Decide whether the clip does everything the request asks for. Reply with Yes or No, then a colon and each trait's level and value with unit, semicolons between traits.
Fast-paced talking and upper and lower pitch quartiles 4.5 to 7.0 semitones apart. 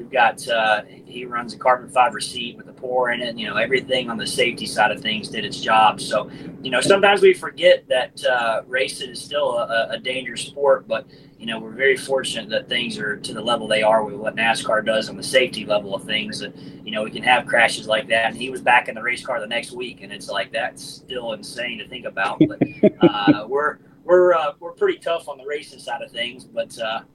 Yes: fast, 245 wpm; wide, 5.6 semitones